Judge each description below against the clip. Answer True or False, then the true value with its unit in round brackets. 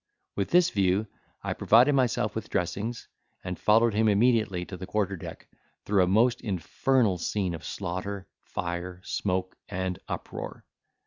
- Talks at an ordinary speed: True (145 wpm)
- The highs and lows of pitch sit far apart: False (3.4 semitones)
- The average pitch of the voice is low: True (100 Hz)